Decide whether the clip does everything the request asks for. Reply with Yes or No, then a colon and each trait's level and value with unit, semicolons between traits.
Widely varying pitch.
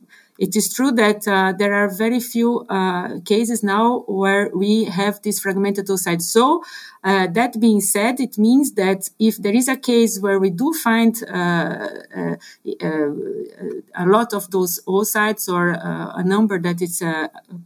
No: average, 3.2 semitones